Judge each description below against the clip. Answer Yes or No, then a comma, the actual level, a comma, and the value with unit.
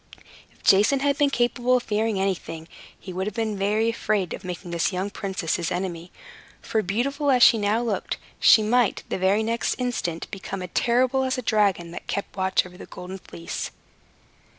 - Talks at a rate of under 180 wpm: No, average, 185 wpm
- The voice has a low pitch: No, high, 205 Hz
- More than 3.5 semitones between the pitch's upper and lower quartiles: Yes, average, 4.4 semitones